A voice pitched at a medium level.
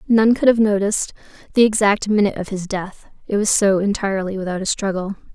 No: high, 200 Hz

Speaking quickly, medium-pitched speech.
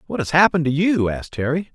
Yes: fast, 240 wpm; medium, 150 Hz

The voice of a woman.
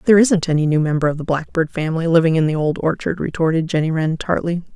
Yes: female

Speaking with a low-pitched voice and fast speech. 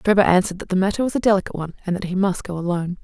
No: medium, 185 Hz; fast, 295 wpm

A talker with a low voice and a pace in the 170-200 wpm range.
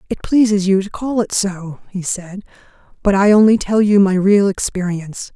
No: high, 195 Hz; average, 190 wpm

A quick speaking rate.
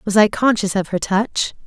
Yes: fast, 215 wpm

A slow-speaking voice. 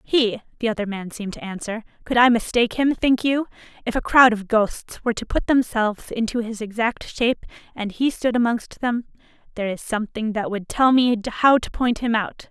No: fast, 205 wpm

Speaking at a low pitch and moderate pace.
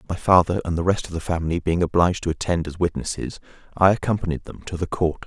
No: very low, 85 Hz; fast, 230 wpm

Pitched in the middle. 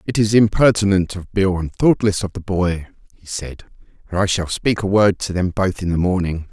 No: very low, 95 Hz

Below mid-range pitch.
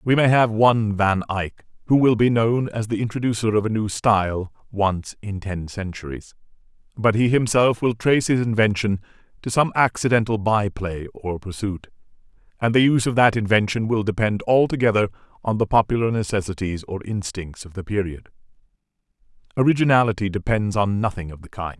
Yes: low, 105 Hz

